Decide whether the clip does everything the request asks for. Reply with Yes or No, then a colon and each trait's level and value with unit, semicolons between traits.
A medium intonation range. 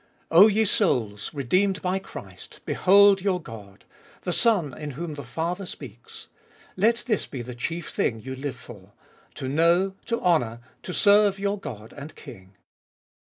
No: wide, 7.9 semitones